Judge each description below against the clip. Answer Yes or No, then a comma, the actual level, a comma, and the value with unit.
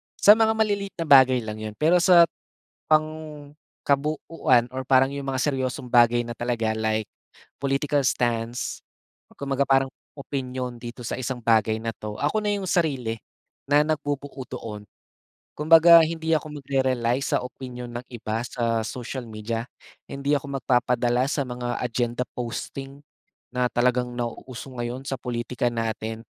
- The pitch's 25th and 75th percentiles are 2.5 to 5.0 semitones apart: Yes, average, 3.1 semitones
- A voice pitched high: No, low, 130 Hz